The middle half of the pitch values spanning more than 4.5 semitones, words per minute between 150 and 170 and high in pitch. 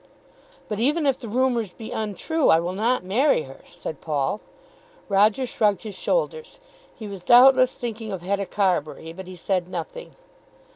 Yes: wide, 5.5 semitones; average, 160 wpm; high, 210 Hz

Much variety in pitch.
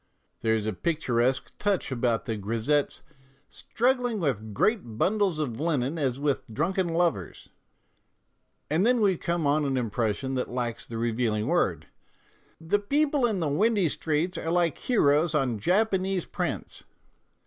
Yes: wide, 7.7 semitones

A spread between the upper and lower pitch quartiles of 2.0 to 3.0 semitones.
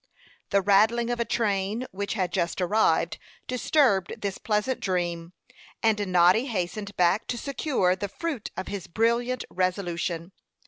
No: average, 4.3 semitones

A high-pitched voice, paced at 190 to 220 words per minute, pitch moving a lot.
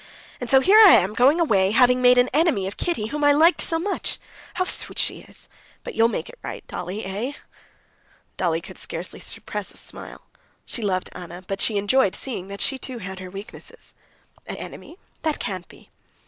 Yes: high, 230 Hz; average, 200 wpm; wide, 7.2 semitones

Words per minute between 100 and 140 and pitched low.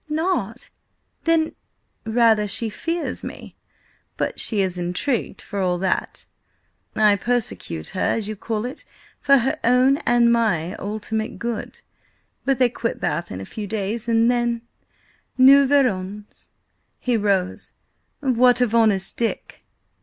No: slow, 135 wpm; high, 225 Hz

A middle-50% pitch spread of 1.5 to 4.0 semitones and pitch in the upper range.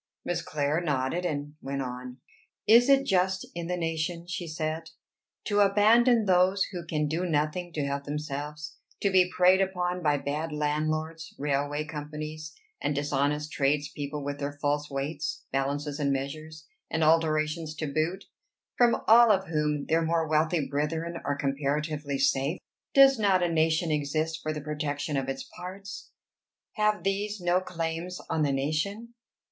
No: average, 3.4 semitones; medium, 155 Hz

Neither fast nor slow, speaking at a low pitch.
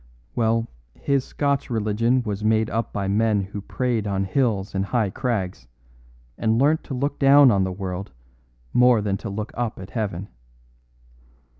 Yes: average, 160 wpm; low, 110 Hz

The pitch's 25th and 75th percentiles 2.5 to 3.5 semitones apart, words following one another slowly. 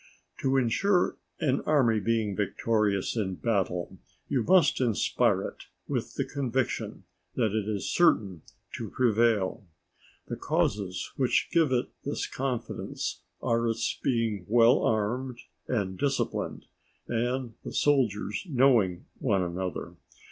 No: average, 4.2 semitones; slow, 125 wpm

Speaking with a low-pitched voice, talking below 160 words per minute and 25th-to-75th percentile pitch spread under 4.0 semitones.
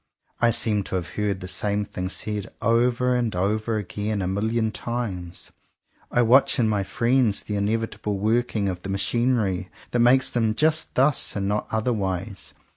No: low, 110 Hz; average, 165 wpm; average, 3.1 semitones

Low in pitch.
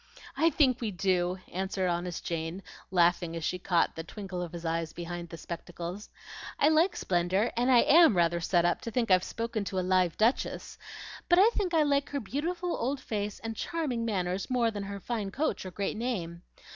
No: high, 195 Hz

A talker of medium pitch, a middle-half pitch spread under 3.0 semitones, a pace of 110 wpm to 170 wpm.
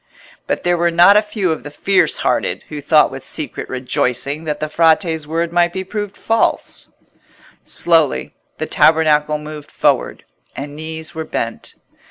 Yes: medium, 160 Hz; narrow, 2.6 semitones; average, 160 wpm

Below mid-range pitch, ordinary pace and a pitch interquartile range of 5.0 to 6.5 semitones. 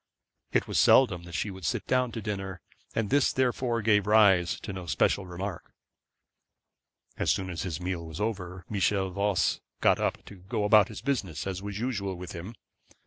No: low, 100 Hz; average, 190 wpm; average, 3.1 semitones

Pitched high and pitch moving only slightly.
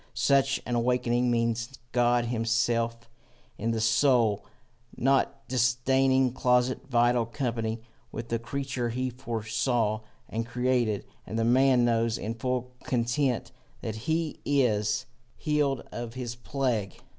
No: low, 120 Hz; narrow, 2.1 semitones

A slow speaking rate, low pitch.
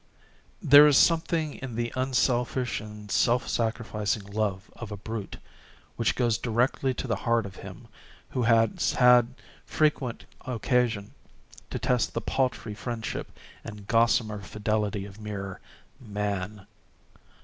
Yes: slow, 125 wpm; low, 115 Hz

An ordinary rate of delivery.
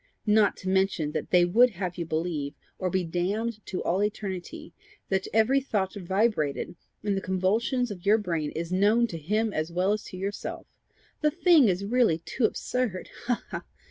Yes: average, 185 wpm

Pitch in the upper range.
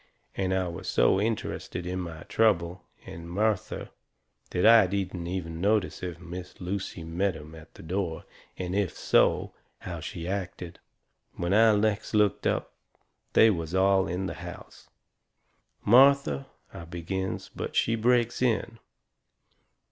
No: very low, 95 Hz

